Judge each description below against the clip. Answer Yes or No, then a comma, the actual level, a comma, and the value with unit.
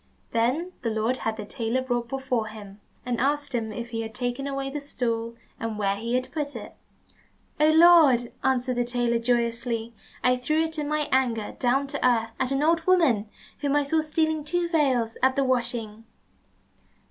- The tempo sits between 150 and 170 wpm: No, average, 185 wpm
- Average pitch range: Yes, average, 3.8 semitones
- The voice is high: Yes, very high, 250 Hz